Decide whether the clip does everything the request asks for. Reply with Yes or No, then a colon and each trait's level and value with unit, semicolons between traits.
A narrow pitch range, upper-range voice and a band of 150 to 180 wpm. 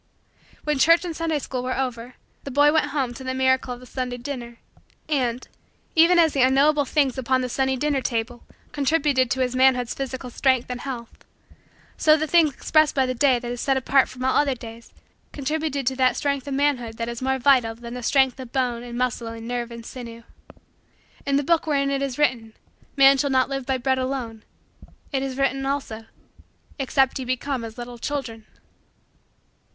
No: narrow, 2.3 semitones; very high, 260 Hz; average, 195 wpm